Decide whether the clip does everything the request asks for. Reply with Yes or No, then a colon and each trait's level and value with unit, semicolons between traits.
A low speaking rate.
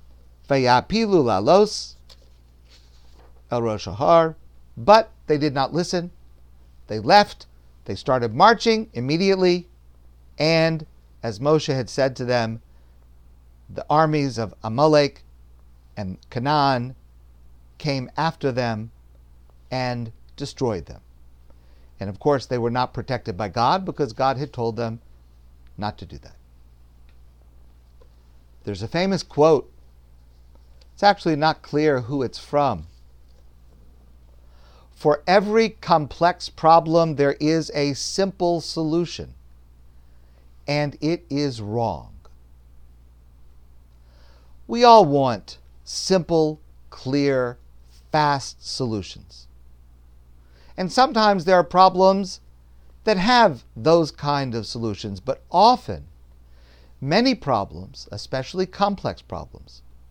Yes: slow, 100 wpm